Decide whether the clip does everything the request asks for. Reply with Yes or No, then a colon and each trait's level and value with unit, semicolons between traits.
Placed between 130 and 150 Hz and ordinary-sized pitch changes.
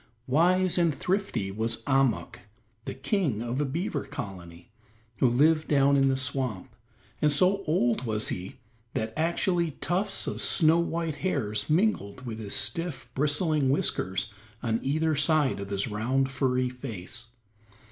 No: low, 135 Hz; wide, 6.0 semitones